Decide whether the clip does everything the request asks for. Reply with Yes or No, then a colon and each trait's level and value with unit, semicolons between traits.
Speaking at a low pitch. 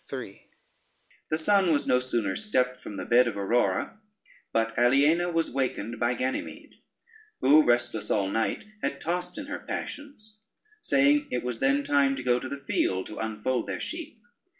Yes: low, 130 Hz